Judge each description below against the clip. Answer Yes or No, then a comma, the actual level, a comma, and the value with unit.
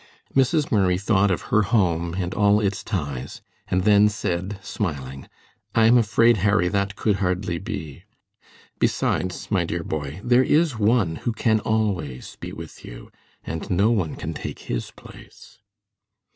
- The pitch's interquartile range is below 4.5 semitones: Yes, average, 4.1 semitones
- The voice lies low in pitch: Yes, low, 100 Hz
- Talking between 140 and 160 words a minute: Yes, average, 155 wpm